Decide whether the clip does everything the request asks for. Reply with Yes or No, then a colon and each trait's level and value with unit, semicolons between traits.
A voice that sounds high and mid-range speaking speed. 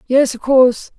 Yes: very high, 255 Hz; average, 180 wpm